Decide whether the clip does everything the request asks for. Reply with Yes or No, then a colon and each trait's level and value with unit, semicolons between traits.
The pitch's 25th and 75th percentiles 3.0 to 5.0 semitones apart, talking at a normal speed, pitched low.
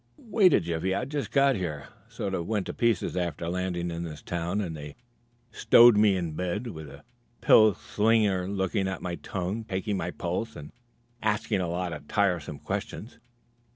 Yes: average, 3.7 semitones; average, 180 wpm; very low, 95 Hz